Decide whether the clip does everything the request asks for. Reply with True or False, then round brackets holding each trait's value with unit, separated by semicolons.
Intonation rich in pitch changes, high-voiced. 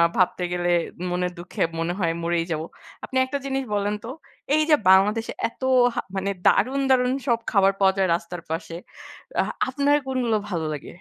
True (6.1 semitones; 195 Hz)